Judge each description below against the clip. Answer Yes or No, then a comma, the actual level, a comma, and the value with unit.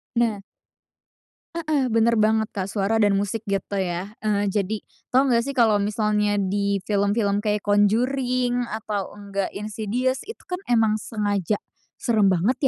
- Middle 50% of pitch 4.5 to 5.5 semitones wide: No, narrow, 2.6 semitones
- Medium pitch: No, high, 210 Hz